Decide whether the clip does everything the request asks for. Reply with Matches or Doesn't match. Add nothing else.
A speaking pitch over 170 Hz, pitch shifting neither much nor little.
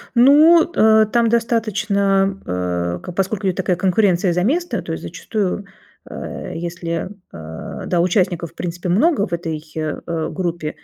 Matches